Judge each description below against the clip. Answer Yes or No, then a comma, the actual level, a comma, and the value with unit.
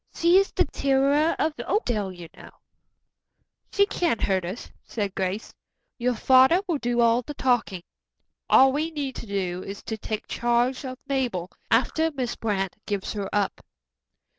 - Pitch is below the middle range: No, high, 240 Hz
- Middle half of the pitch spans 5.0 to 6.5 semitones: Yes, wide, 5.6 semitones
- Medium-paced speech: Yes, average, 160 wpm